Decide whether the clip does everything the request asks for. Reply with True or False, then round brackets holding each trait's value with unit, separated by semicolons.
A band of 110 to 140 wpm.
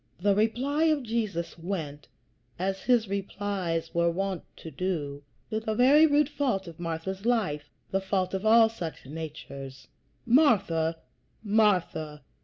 True (135 wpm)